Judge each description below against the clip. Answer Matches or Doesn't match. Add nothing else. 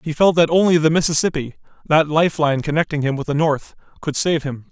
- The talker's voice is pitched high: Doesn't match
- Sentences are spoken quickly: Matches